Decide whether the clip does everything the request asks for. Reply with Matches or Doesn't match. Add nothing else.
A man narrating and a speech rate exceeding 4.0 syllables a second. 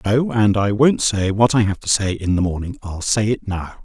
Matches